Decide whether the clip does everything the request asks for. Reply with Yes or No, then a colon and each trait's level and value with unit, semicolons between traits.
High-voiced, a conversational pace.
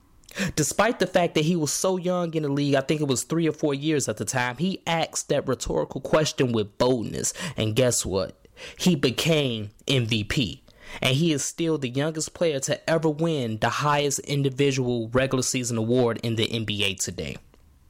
No: low, 135 Hz; average, 185 wpm